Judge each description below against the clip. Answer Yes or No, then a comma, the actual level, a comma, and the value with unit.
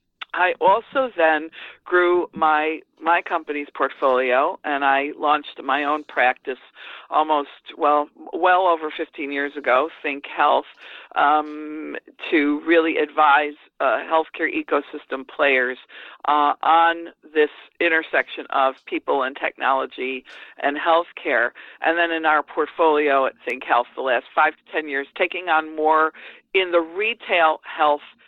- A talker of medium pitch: Yes, medium, 155 Hz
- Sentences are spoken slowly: Yes, slow, 130 wpm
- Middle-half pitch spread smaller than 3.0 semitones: Yes, narrow, 2.4 semitones